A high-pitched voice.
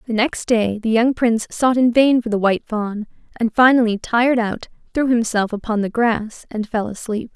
Yes: high, 225 Hz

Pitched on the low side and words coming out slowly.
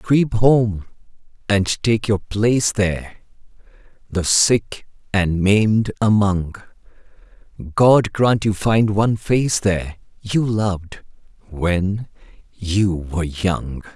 Yes: low, 100 Hz; slow, 110 wpm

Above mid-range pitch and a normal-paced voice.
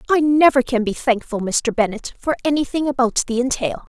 Yes: very high, 250 Hz; average, 180 wpm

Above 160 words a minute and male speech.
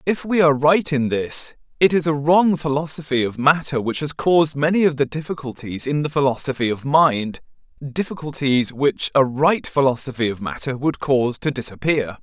Yes: average, 170 wpm; male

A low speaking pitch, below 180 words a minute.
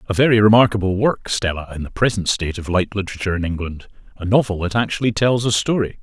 No: low, 100 Hz; average, 200 wpm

